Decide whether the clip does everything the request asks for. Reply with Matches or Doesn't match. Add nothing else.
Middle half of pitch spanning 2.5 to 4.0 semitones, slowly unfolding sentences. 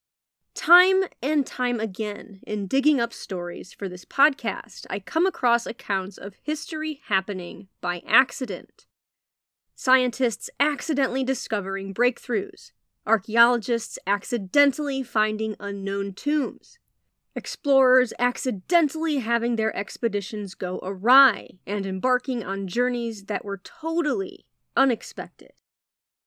Doesn't match